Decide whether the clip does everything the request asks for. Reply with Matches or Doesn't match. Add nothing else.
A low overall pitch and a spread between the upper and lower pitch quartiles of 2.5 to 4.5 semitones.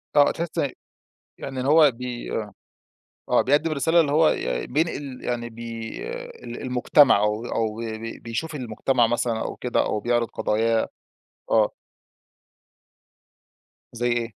Matches